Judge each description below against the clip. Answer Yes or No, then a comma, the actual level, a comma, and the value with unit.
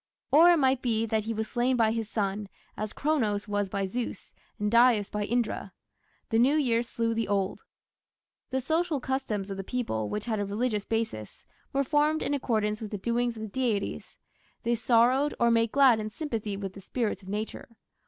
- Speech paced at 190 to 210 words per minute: Yes, average, 200 wpm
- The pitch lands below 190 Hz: No, high, 230 Hz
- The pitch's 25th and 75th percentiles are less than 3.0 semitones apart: No, average, 3.4 semitones